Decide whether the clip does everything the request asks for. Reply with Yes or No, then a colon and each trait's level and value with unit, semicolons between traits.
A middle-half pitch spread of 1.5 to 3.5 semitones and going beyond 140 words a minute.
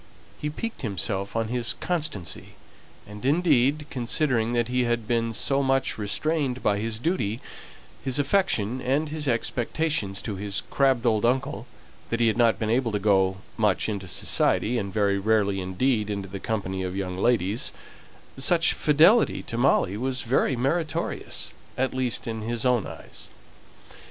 No: average, 4.5 semitones; average, 155 wpm